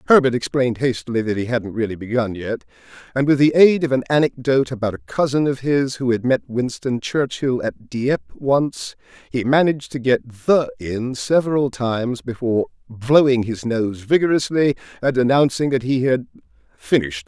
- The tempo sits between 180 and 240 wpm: No, average, 165 wpm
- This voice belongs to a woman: No, male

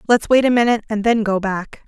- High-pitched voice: Yes, high, 220 Hz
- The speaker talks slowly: No, fast, 290 wpm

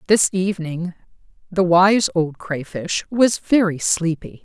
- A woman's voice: Yes, female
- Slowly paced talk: Yes, slow, 120 wpm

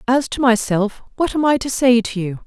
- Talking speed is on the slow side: No, fast, 245 wpm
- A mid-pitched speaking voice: No, high, 240 Hz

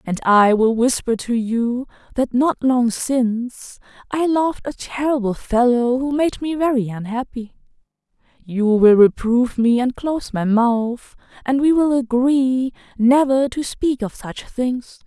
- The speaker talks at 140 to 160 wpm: Yes, average, 150 wpm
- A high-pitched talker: Yes, high, 245 Hz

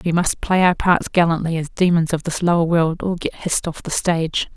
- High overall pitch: No, medium, 170 Hz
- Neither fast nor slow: No, fast, 235 wpm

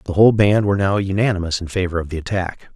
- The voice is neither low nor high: No, very low, 95 Hz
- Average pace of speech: No, fast, 240 wpm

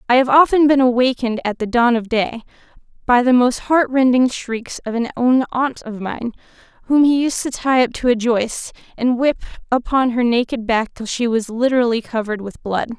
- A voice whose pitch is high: Yes, high, 245 Hz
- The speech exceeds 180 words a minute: Yes, fast, 205 wpm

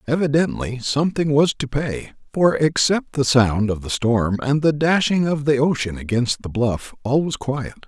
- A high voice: No, low, 135 Hz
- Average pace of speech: Yes, average, 185 wpm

